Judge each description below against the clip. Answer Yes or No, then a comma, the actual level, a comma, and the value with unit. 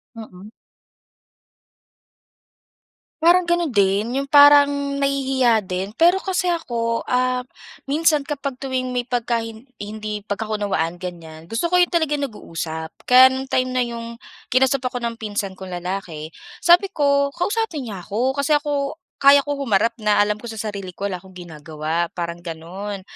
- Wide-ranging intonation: Yes, wide, 6.3 semitones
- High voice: Yes, high, 235 Hz